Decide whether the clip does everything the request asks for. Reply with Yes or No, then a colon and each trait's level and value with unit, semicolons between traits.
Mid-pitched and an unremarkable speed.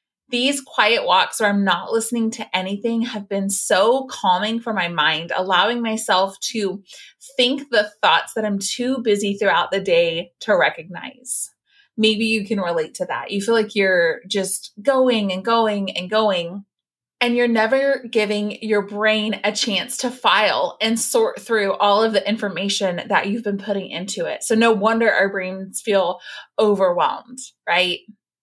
No: high, 210 Hz; average, 165 wpm